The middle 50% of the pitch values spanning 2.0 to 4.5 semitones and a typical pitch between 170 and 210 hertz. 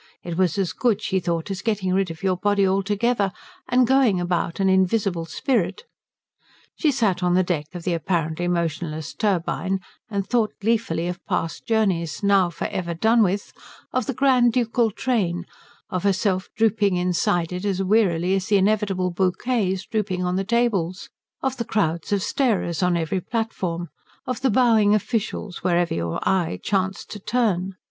Yes: average, 3.8 semitones; high, 190 Hz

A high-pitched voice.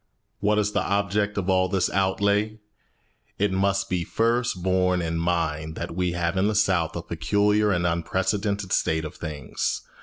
No: very low, 95 Hz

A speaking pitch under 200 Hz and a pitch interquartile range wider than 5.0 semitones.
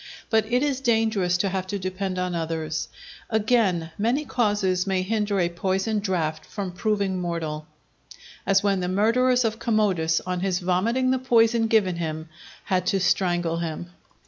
No: high, 190 Hz; average, 3.8 semitones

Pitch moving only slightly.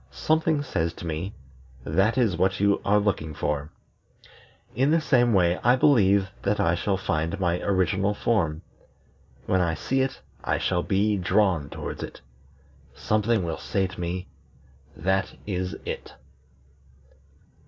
No: average, 3.7 semitones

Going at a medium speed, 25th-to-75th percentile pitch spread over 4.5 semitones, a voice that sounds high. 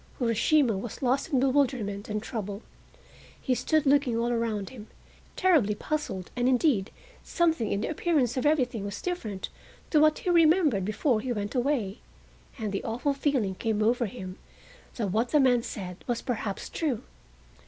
Yes: average, 165 wpm; average, 5.3 semitones; high, 245 Hz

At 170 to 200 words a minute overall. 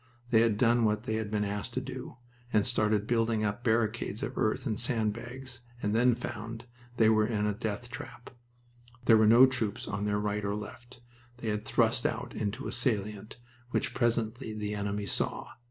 Yes: average, 190 wpm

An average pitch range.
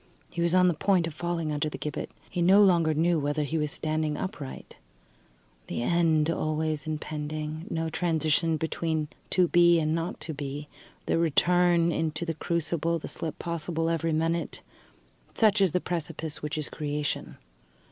No: narrow, 1.9 semitones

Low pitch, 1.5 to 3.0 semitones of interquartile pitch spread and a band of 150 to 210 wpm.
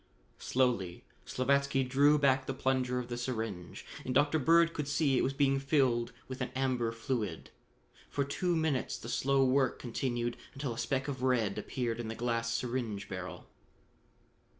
Yes: low, 130 Hz; average, 2.7 semitones; average, 165 wpm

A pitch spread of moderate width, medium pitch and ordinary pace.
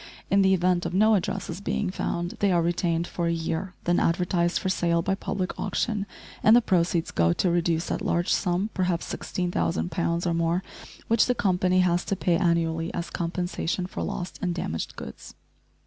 No: narrow, 1.8 semitones; medium, 175 Hz; average, 185 wpm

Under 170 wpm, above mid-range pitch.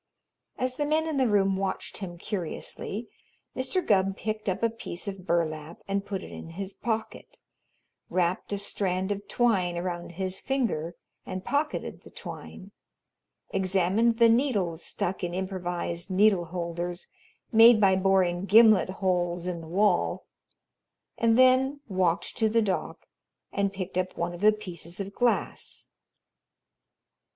Yes: average, 145 wpm; high, 195 Hz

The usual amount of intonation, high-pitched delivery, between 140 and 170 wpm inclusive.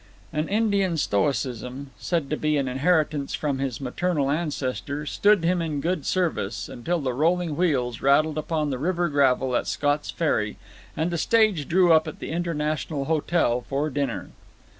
No: average, 3.9 semitones; medium, 150 Hz; average, 160 wpm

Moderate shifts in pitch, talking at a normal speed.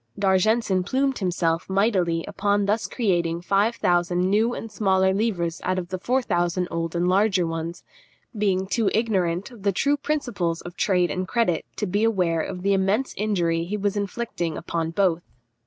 Yes: average, 3.4 semitones; average, 170 wpm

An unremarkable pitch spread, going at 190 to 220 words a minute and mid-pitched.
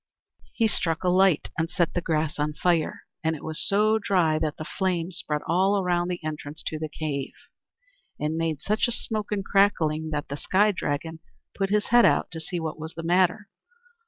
Yes: average, 3.6 semitones; average, 200 wpm; medium, 165 Hz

